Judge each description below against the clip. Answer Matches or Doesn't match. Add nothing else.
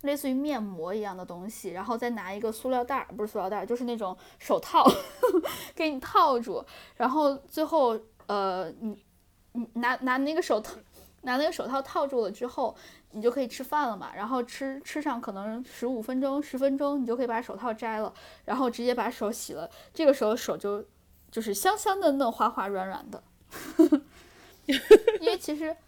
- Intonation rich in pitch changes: Doesn't match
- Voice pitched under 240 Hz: Doesn't match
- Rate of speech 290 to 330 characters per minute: Doesn't match